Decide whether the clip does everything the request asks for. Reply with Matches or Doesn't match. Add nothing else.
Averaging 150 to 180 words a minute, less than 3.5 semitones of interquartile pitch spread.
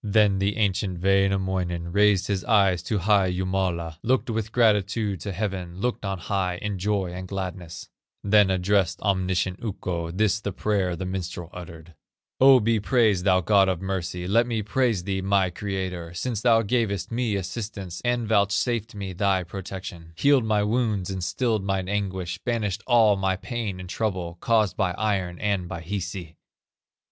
Matches